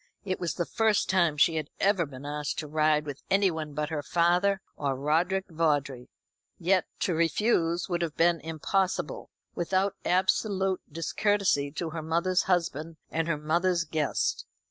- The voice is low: No, medium, 165 Hz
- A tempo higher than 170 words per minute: No, average, 155 wpm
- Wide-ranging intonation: No, average, 3.5 semitones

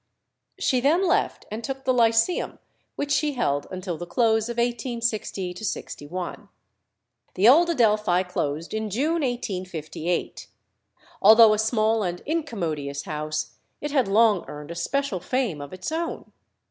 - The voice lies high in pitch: Yes, high, 220 Hz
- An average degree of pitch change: No, wide, 6.1 semitones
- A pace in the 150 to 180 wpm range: No, average, 140 wpm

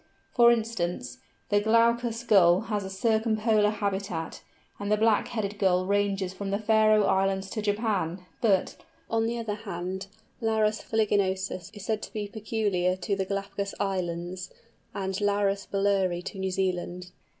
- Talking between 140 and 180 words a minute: Yes, average, 150 wpm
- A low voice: No, high, 200 Hz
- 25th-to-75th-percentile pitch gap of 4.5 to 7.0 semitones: No, narrow, 2.4 semitones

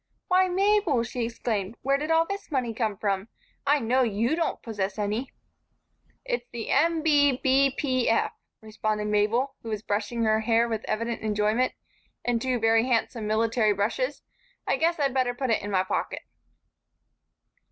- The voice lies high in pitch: Yes, high, 235 Hz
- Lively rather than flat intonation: No, average, 4.2 semitones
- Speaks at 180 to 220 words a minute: No, average, 165 wpm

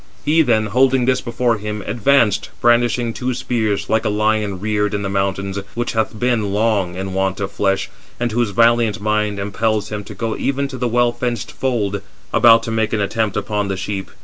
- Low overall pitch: Yes, low, 110 Hz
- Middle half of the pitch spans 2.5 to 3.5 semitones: Yes, average, 2.8 semitones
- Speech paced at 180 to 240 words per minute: Yes, average, 200 wpm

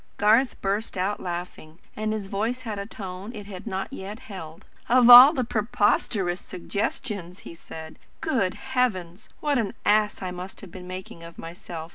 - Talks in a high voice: Yes, high, 200 Hz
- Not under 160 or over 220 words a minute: Yes, average, 170 wpm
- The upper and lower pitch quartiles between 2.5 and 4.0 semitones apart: Yes, average, 3.6 semitones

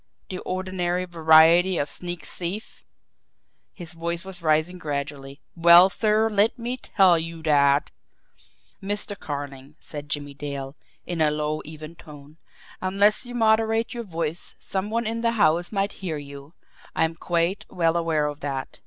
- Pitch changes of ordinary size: Yes, average, 4.3 semitones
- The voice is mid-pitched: Yes, medium, 170 Hz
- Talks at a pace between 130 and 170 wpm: Yes, average, 155 wpm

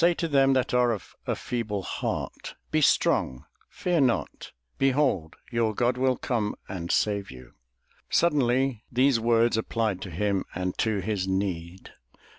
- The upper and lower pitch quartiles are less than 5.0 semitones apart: No, average, 5.3 semitones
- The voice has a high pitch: No, low, 115 Hz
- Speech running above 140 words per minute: Yes, average, 150 wpm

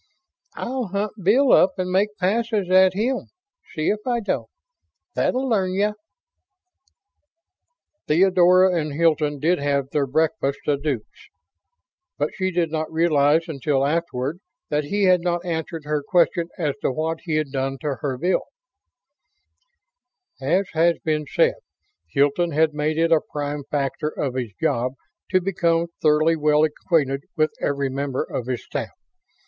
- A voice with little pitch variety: No, average, 4.1 semitones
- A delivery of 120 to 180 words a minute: Yes, average, 150 wpm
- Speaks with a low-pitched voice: No, medium, 160 Hz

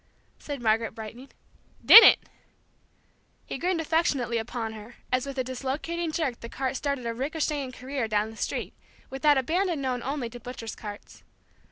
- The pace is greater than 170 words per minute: No, average, 160 wpm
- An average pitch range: Yes, average, 3.8 semitones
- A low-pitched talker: No, very high, 260 Hz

